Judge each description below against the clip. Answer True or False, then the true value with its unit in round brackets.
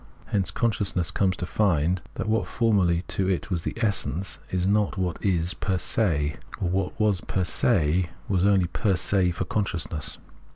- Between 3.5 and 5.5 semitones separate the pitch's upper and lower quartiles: False (2.7 semitones)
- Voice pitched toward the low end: True (95 Hz)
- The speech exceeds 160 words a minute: True (170 wpm)